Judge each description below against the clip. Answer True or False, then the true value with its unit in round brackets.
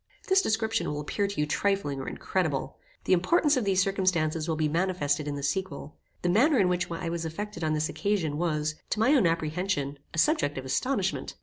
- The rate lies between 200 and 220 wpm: True (205 wpm)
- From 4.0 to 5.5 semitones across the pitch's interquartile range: True (4.8 semitones)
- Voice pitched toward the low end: False (175 Hz)